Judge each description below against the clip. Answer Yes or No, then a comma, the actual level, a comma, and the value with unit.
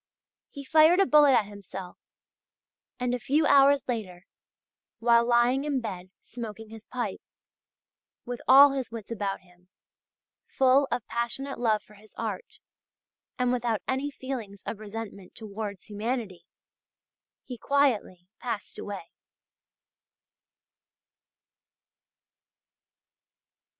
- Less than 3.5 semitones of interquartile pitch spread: No, average, 4.2 semitones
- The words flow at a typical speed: No, slow, 110 wpm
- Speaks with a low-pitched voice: No, high, 235 Hz